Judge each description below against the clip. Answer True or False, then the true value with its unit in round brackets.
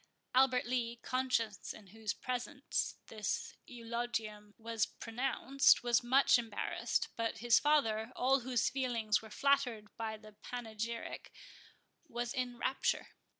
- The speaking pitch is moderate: False (235 Hz)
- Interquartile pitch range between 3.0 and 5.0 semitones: False (2.5 semitones)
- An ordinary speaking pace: False (120 wpm)